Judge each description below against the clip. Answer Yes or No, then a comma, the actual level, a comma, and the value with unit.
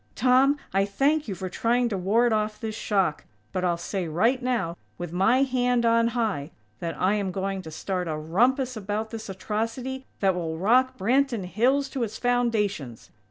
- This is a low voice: No, high, 215 Hz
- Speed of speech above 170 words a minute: Yes, average, 180 wpm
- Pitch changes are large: No, average, 4.7 semitones